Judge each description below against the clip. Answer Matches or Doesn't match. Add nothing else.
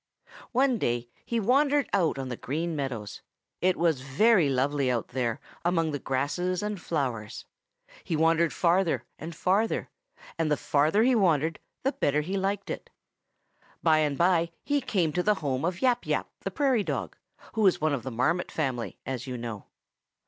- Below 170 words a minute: Doesn't match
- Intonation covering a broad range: Matches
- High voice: Doesn't match